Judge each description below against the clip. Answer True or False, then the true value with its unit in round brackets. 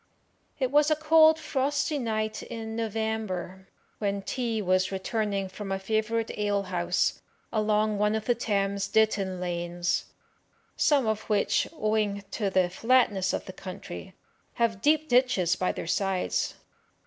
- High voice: True (215 Hz)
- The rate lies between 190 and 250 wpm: False (140 wpm)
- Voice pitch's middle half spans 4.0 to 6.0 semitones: False (3.2 semitones)